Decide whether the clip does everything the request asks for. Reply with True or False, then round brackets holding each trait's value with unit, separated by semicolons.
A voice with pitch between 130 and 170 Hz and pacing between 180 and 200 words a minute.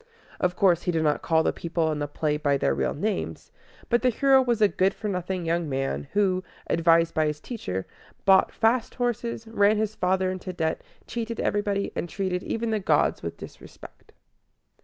False (185 Hz; 190 wpm)